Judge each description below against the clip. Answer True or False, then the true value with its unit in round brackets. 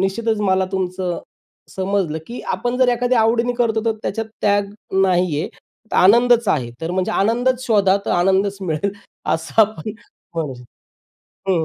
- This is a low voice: False (200 Hz)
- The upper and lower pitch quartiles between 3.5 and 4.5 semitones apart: True (4.0 semitones)